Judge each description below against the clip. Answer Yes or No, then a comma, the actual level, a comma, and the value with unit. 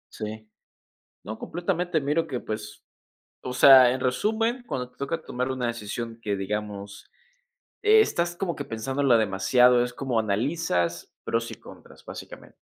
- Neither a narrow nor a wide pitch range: No, wide, 5.9 semitones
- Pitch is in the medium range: No, low, 125 Hz